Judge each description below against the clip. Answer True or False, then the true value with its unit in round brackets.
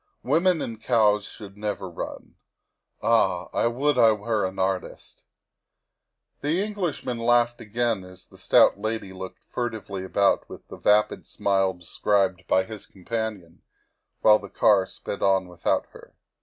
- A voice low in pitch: True (105 Hz)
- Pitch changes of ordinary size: True (3.6 semitones)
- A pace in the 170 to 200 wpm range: False (150 wpm)